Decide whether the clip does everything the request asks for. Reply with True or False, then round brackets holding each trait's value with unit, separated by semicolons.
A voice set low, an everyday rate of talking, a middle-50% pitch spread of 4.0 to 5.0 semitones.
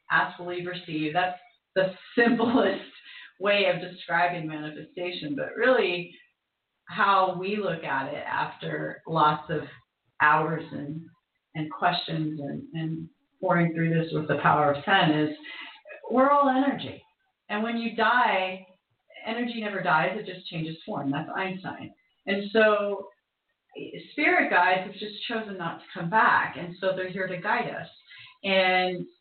False (185 Hz; 145 wpm; 4.6 semitones)